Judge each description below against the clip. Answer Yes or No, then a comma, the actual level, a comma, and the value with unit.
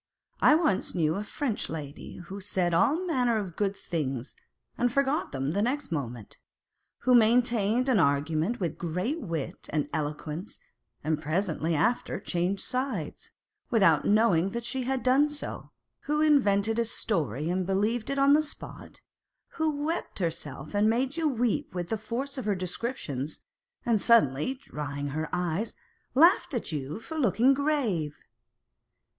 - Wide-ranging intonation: Yes, wide, 7.9 semitones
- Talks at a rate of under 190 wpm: Yes, average, 150 wpm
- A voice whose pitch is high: Yes, high, 205 Hz